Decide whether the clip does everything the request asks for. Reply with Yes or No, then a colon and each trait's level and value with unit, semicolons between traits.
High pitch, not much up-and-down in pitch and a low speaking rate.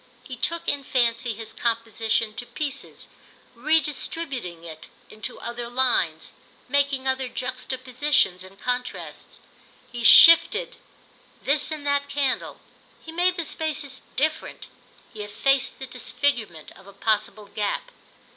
No: very high, 255 Hz; average, 4.2 semitones; slow, 120 wpm